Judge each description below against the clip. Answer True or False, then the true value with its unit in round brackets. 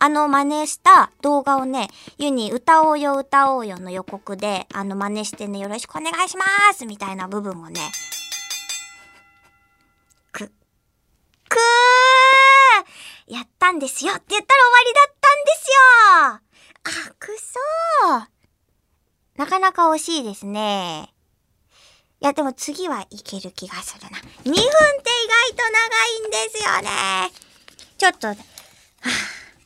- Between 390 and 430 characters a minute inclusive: False (250 characters per minute)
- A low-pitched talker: False (275 Hz)